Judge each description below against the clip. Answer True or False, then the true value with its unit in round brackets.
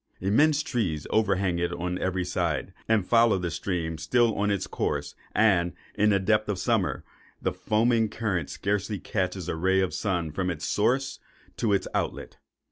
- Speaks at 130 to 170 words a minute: False (180 wpm)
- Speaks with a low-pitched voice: True (100 Hz)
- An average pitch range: True (3.5 semitones)